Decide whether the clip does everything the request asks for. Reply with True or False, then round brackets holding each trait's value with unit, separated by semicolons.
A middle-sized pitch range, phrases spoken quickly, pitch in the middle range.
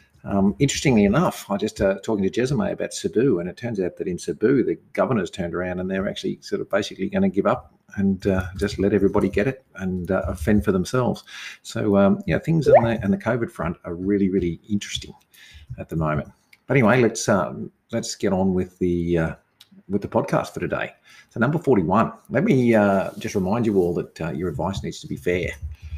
False (3.6 semitones; 220 wpm; 100 Hz)